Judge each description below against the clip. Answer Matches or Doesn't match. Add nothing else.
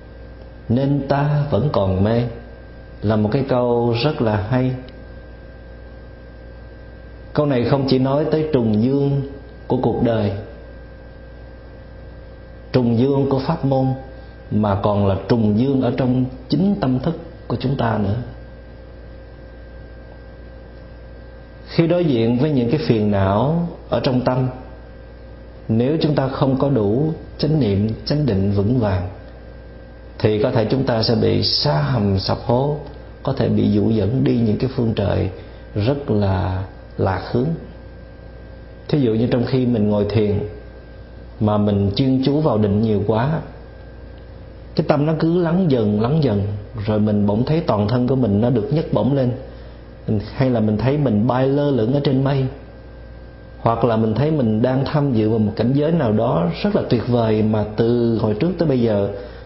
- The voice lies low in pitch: Matches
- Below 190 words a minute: Matches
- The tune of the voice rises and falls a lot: Doesn't match